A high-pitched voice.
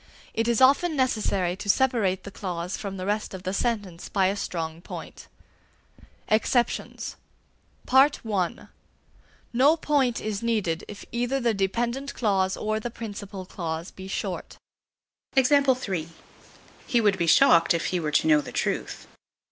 Yes: high, 205 Hz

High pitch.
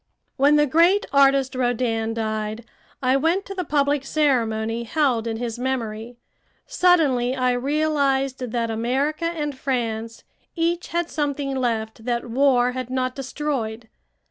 Yes: very high, 260 Hz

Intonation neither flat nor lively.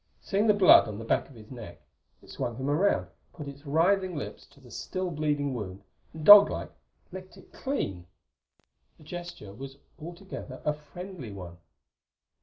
No: wide, 7.3 semitones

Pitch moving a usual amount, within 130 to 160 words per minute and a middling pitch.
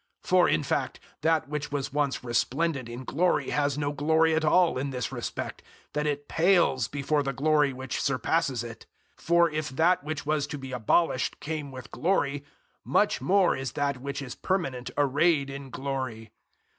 No: average, 3.1 semitones; average, 180 wpm; medium, 145 Hz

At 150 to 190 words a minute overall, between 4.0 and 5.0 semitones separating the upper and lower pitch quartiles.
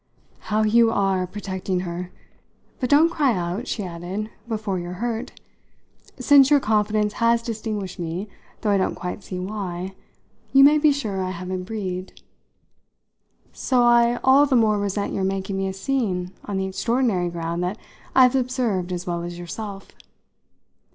Yes: average, 160 wpm; average, 4.3 semitones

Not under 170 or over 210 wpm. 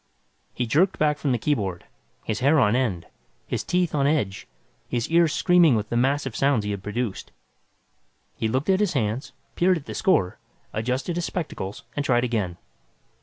Yes: average, 180 wpm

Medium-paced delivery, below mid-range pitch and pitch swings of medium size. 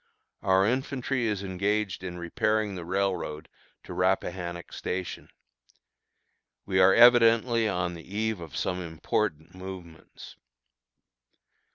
No: slow, 105 wpm; very low, 95 Hz; average, 3.4 semitones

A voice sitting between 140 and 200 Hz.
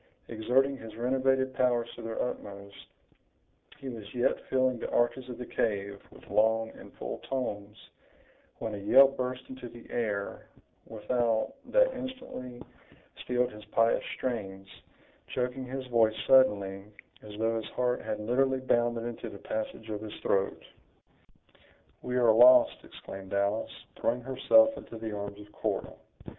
No: low, 120 Hz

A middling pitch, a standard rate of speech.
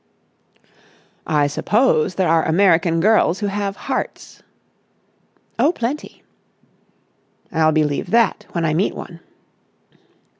No: medium, 175 Hz; slow, 105 wpm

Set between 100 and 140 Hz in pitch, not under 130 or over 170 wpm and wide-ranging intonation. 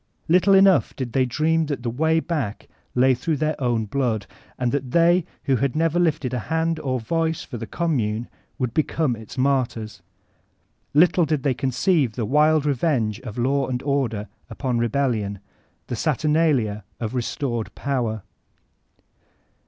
No: low, 135 Hz; average, 150 wpm; average, 4.8 semitones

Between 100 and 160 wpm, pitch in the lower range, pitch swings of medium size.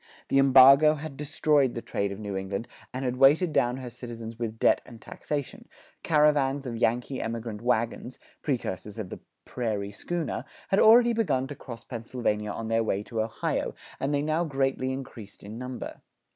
No: average, 170 wpm; low, 125 Hz; average, 4.0 semitones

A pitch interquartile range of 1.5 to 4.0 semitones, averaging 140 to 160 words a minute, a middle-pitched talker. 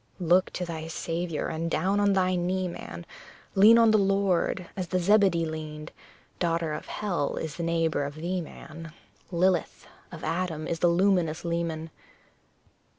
Yes: narrow, 2.4 semitones; average, 150 wpm; medium, 170 Hz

